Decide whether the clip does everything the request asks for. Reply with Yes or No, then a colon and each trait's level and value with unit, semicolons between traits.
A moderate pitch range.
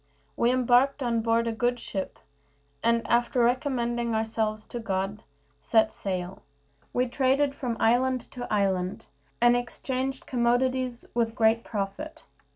No: narrow, 2.3 semitones